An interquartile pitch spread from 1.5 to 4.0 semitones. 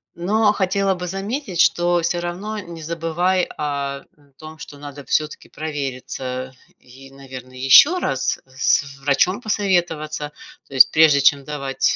No: average, 4.6 semitones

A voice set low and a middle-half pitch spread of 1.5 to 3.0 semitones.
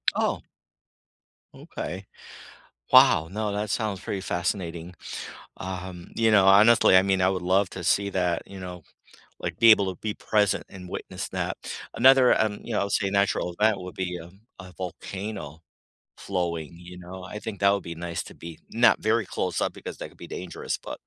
Yes: very low, 95 Hz; narrow, 2.4 semitones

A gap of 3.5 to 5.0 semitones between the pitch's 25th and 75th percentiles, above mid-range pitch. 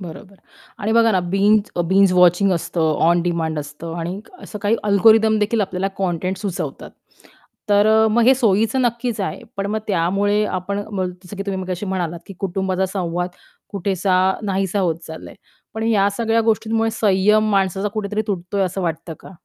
No: average, 2.8 semitones; high, 195 Hz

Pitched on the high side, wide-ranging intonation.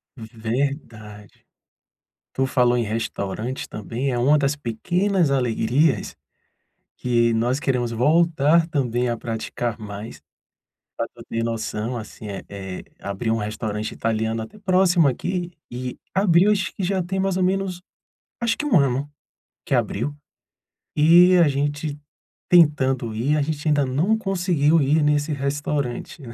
No: medium, 140 Hz; wide, 6.4 semitones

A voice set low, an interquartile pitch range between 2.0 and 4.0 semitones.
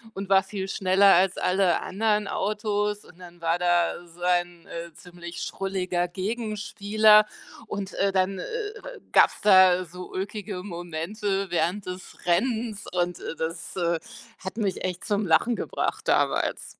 No: high, 190 Hz; average, 2.8 semitones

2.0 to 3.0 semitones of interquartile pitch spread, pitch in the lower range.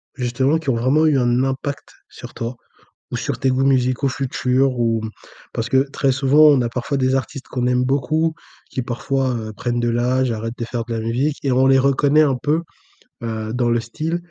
Yes: narrow, 2.4 semitones; low, 130 Hz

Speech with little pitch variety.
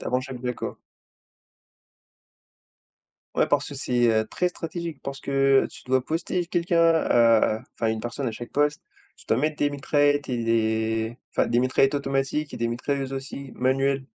No: average, 3.4 semitones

